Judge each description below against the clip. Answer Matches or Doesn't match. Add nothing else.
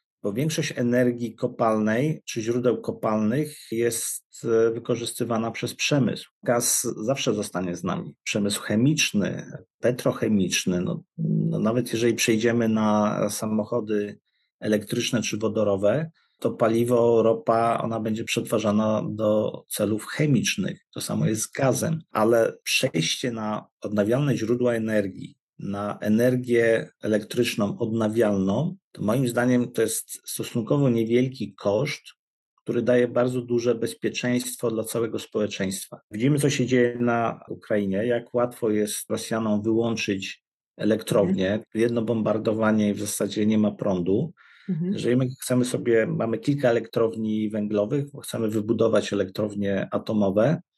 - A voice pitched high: Doesn't match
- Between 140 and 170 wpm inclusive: Doesn't match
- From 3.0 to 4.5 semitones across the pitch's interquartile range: Doesn't match